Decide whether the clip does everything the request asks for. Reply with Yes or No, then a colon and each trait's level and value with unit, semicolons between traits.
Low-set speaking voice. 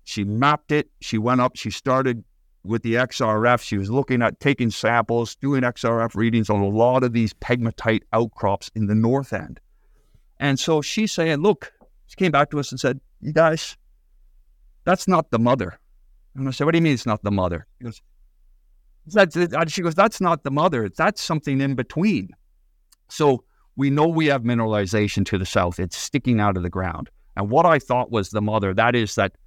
Yes: low, 120 Hz